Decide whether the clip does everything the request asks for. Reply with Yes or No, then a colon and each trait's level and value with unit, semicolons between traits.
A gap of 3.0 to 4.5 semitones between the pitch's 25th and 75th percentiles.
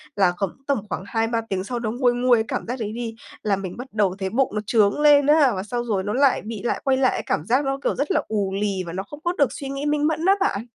No: average, 5.1 semitones